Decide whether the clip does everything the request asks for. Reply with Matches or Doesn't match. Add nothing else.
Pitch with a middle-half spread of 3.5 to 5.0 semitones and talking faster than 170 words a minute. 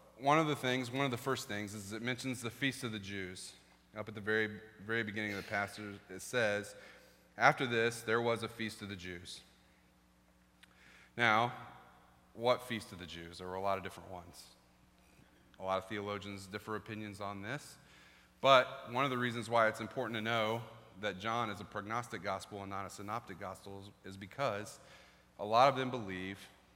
Matches